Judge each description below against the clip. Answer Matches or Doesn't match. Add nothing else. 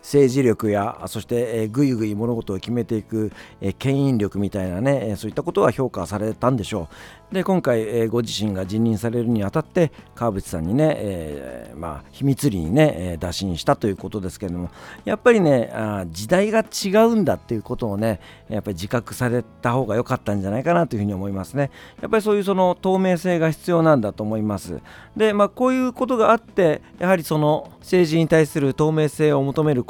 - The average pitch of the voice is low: Matches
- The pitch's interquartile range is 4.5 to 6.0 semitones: Doesn't match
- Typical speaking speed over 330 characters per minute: Matches